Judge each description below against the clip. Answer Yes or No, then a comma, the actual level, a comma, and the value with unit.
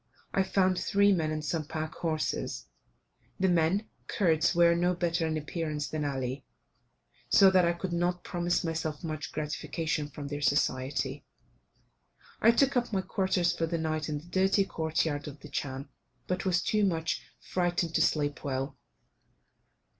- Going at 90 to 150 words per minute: No, average, 160 wpm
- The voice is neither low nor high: Yes, medium, 165 Hz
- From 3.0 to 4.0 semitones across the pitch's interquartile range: Yes, average, 3.3 semitones